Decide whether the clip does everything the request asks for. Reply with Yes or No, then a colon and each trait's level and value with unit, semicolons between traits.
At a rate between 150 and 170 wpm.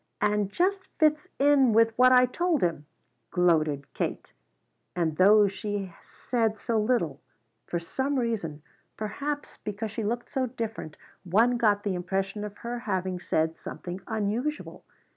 No: average, 140 wpm